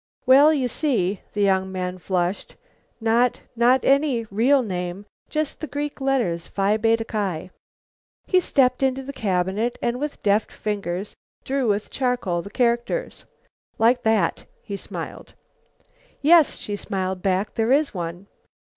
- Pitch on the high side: Yes, high, 225 Hz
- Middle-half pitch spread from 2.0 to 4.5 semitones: No, wide, 5.6 semitones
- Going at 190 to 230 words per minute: No, average, 140 wpm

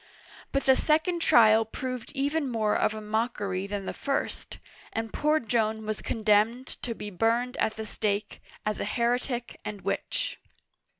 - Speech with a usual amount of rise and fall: Yes, average, 3.0 semitones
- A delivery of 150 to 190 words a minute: Yes, average, 160 wpm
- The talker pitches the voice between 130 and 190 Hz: No, high, 225 Hz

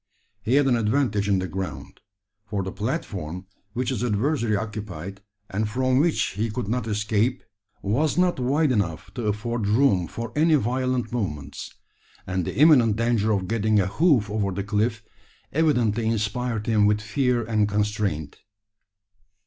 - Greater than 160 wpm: No, average, 155 wpm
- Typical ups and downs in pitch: Yes, average, 3.5 semitones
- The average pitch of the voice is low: Yes, low, 110 Hz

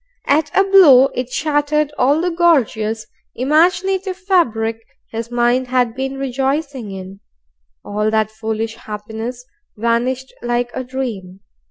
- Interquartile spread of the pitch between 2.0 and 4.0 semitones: No, average, 4.8 semitones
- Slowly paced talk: Yes, slow, 125 wpm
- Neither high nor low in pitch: No, very high, 250 Hz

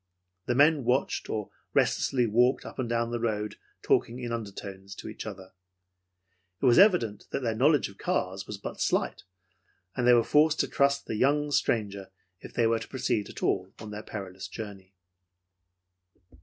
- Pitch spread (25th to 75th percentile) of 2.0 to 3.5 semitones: No, average, 4.0 semitones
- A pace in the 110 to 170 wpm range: No, average, 180 wpm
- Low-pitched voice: Yes, low, 115 Hz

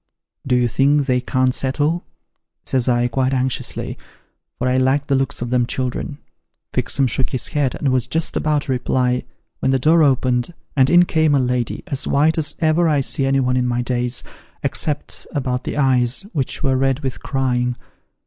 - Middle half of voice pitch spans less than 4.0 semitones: Yes, narrow, 2.4 semitones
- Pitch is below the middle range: Yes, low, 130 Hz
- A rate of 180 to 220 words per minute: Yes, average, 190 wpm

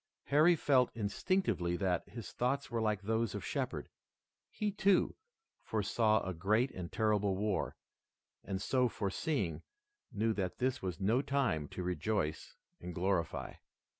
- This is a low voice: Yes, low, 105 Hz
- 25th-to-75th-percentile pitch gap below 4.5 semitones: No, average, 5.2 semitones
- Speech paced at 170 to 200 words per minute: No, slow, 135 wpm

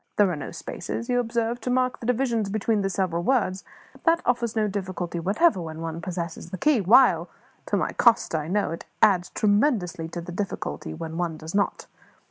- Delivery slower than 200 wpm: No, fast, 205 wpm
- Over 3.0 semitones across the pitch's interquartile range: Yes, wide, 5.4 semitones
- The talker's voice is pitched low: No, high, 195 Hz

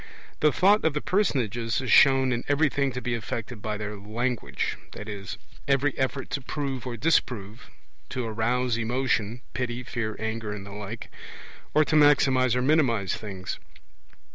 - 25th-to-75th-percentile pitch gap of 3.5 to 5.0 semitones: Yes, average, 3.8 semitones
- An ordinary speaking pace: Yes, average, 155 wpm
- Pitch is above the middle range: No, low, 125 Hz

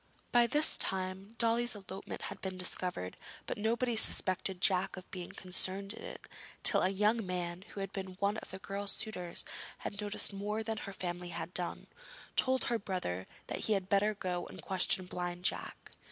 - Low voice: No, high, 195 Hz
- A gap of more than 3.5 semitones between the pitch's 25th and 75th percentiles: No, narrow, 2.5 semitones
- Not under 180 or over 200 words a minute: Yes, average, 185 wpm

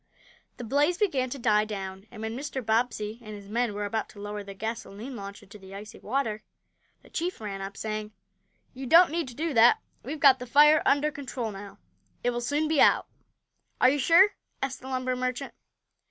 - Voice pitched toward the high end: Yes, high, 240 Hz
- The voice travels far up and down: No, average, 4.8 semitones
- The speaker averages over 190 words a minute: Yes, average, 200 wpm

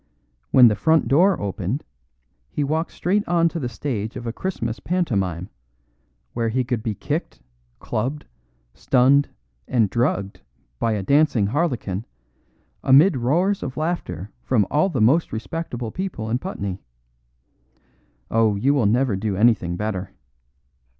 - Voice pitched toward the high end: No, low, 120 Hz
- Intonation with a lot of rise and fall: Yes, wide, 6.3 semitones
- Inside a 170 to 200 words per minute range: No, slow, 135 wpm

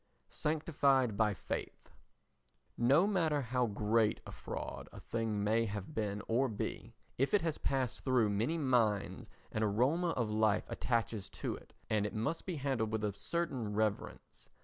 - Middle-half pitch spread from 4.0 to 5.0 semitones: Yes, average, 4.5 semitones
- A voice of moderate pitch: No, low, 115 Hz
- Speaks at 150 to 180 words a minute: Yes, average, 160 wpm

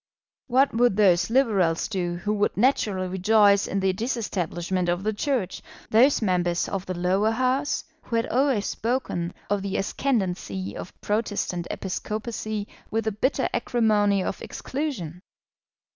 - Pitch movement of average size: Yes, average, 4.1 semitones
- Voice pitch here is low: No, high, 205 Hz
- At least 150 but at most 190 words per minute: No, average, 140 wpm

